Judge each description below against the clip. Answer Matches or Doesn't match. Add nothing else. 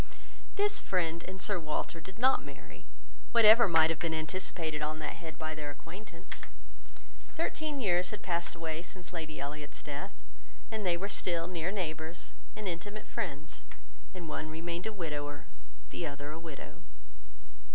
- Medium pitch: Matches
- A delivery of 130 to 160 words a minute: Matches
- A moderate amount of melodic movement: Matches